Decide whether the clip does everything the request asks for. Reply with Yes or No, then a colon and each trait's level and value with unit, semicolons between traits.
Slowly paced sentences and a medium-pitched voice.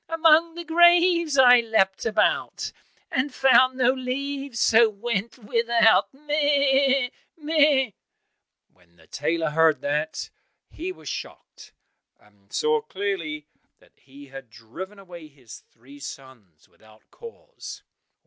No: slow, 120 wpm; high, 230 Hz